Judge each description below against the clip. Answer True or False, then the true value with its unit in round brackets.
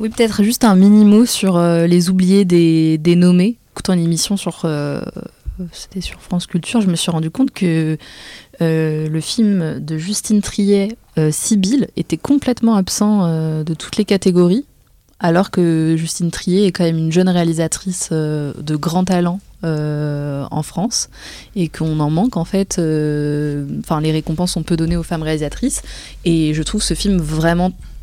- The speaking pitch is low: False (175 Hz)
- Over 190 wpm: False (175 wpm)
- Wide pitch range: False (3.7 semitones)